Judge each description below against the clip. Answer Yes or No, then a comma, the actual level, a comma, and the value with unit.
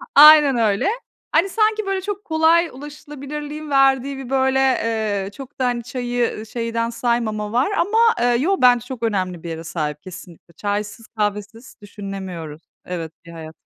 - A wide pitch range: Yes, wide, 5.8 semitones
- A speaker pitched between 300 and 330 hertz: No, high, 240 Hz